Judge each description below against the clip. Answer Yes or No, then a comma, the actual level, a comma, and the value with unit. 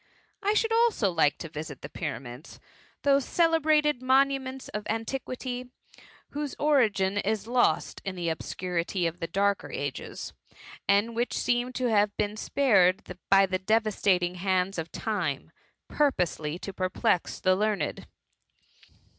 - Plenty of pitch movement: Yes, wide, 6.0 semitones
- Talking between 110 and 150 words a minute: Yes, slow, 135 wpm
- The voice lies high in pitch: Yes, high, 205 Hz